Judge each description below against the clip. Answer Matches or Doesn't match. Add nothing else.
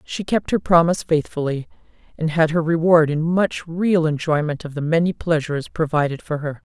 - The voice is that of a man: Doesn't match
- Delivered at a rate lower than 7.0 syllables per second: Matches